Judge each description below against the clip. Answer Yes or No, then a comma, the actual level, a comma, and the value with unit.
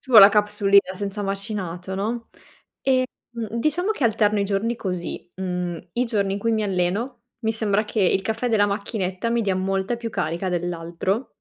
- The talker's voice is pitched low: No, high, 205 Hz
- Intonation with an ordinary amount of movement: Yes, average, 3.2 semitones